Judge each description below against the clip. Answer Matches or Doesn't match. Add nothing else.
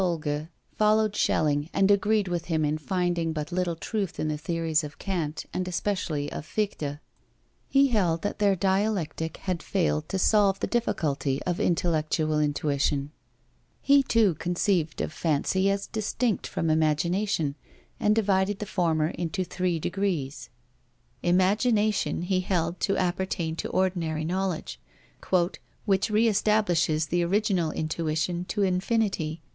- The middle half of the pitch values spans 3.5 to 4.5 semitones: Matches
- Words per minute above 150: Doesn't match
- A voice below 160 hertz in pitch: Doesn't match